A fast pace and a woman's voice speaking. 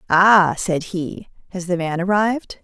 No: average, 160 wpm; female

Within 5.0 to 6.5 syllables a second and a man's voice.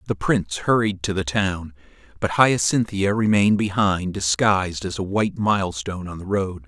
Yes: 5.1 syllables/s; male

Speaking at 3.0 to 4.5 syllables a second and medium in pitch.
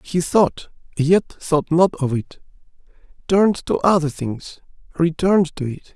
Yes: 4.1 syllables/s; medium, 165 Hz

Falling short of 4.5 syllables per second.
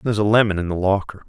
No: 7.8 syllables/s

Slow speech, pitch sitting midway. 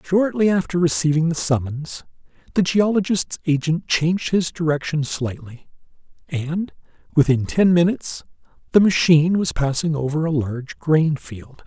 Yes: slow, 130 wpm; medium, 160 Hz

